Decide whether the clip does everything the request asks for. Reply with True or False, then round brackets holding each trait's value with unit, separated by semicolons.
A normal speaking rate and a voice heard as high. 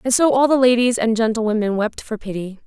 False (225 wpm; 230 Hz)